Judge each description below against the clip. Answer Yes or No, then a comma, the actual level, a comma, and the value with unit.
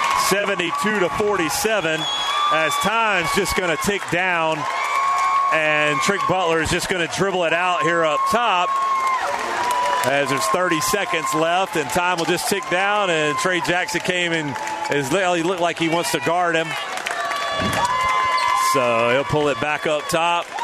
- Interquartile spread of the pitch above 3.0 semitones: Yes, average, 4.2 semitones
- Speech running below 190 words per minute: Yes, average, 160 wpm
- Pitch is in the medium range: Yes, medium, 175 Hz